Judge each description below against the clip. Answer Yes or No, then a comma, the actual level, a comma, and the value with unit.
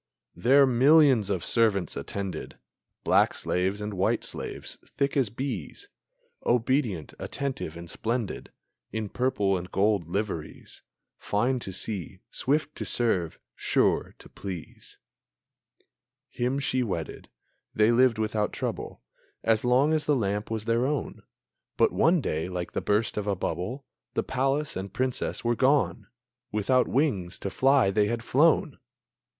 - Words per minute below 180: Yes, average, 140 wpm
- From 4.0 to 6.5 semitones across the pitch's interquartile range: Yes, average, 5.1 semitones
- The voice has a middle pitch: No, low, 115 Hz